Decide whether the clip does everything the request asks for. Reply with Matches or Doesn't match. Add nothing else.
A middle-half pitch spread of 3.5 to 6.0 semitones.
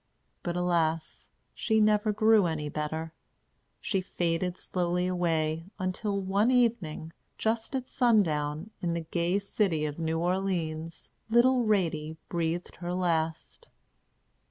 Matches